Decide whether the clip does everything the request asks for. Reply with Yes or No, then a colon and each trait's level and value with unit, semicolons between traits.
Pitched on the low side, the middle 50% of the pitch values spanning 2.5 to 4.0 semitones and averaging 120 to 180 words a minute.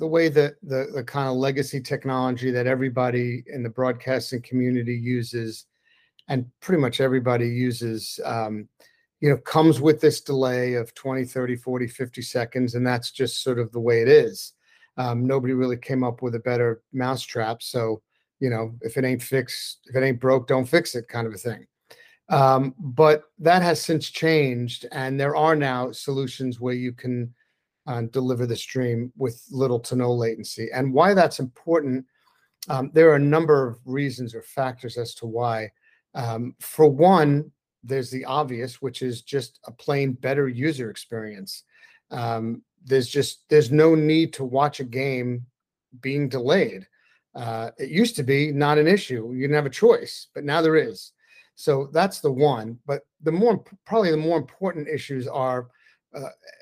Yes: low, 130 Hz; average, 3.4 semitones; average, 175 wpm